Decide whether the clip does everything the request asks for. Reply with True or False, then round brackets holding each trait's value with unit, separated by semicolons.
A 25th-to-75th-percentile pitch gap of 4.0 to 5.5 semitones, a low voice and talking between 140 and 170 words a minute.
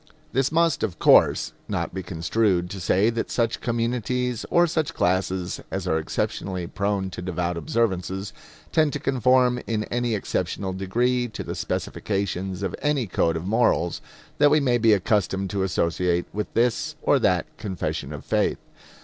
True (4.9 semitones; 100 Hz; 160 wpm)